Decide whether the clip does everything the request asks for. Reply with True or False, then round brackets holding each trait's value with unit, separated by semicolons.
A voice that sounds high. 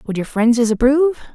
True (250 Hz)